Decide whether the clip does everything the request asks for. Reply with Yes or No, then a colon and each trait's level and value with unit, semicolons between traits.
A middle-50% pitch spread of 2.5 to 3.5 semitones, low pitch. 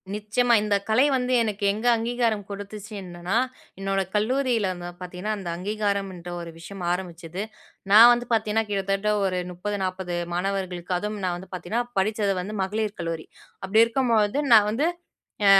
No: average, 3.1 semitones; high, 205 Hz